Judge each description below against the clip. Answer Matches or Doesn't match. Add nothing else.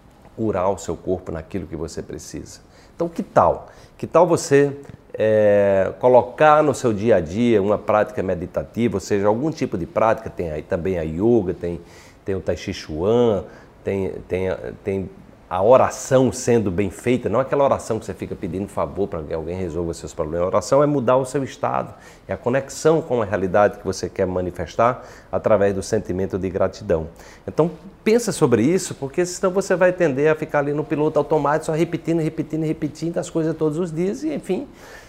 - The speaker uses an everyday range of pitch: Doesn't match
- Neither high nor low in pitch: Doesn't match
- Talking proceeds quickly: Matches